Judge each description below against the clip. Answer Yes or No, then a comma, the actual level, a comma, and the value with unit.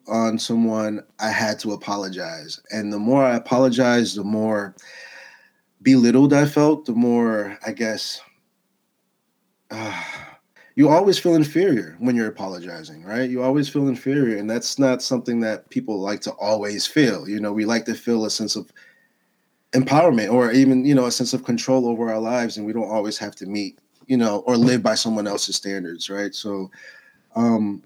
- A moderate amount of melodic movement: Yes, average, 3.3 semitones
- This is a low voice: Yes, low, 115 Hz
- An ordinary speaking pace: Yes, average, 175 wpm